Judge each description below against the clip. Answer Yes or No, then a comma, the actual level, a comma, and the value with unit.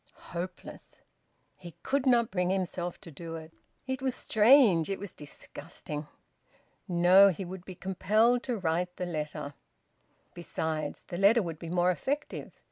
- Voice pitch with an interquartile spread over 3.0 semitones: Yes, average, 4.1 semitones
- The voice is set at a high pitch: No, medium, 180 Hz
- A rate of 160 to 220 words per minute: No, average, 145 wpm